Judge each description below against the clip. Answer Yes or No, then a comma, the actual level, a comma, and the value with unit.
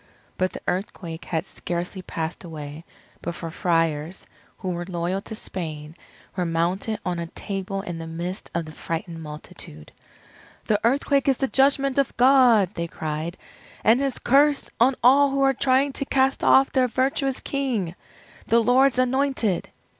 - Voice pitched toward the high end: Yes, high, 195 Hz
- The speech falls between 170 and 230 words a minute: No, average, 155 wpm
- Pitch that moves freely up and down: Yes, wide, 7.8 semitones